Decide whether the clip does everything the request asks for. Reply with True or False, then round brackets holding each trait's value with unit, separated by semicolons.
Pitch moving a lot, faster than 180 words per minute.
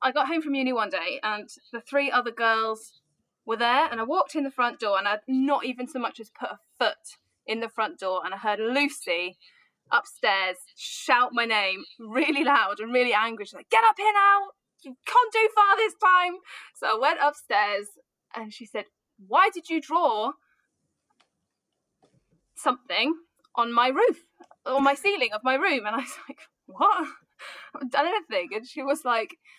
True (6.2 semitones; 190 wpm)